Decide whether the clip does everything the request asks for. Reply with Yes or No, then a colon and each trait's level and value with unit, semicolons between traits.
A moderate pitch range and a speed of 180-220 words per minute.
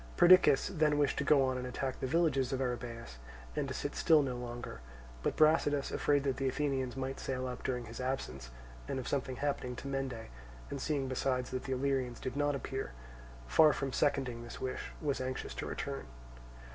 No: narrow, 2.0 semitones; average, 195 wpm